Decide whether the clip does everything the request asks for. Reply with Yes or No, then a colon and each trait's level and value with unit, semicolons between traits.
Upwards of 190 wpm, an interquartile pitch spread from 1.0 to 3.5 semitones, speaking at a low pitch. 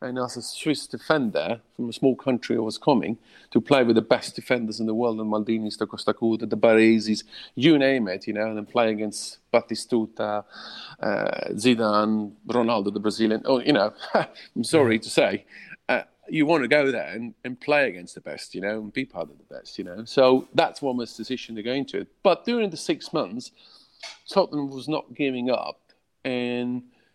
Yes: average, 200 wpm; average, 3.1 semitones; low, 120 Hz